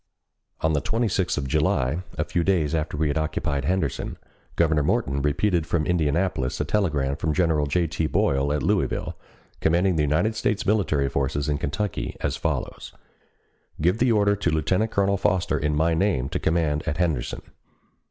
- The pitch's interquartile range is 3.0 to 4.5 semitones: Yes, average, 4.1 semitones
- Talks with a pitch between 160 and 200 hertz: No, very low, 80 Hz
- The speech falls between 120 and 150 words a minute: No, average, 170 wpm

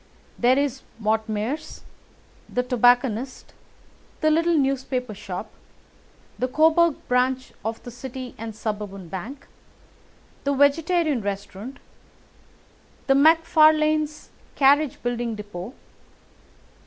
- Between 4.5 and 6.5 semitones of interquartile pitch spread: Yes, average, 5.0 semitones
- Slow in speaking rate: Yes, slow, 95 wpm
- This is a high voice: Yes, very high, 255 Hz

